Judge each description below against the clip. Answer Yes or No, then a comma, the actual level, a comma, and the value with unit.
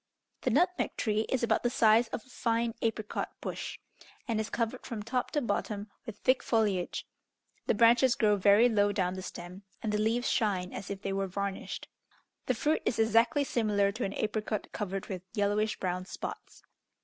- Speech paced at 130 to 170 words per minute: No, average, 185 wpm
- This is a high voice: Yes, high, 215 Hz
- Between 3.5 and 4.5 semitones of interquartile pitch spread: No, average, 2.7 semitones